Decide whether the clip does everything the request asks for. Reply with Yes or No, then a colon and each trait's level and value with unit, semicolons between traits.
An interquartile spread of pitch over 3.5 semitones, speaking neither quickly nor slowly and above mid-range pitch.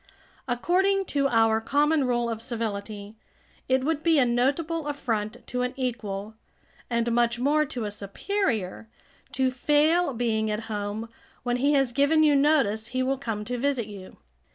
Yes: average, 4.4 semitones; average, 160 wpm; high, 245 Hz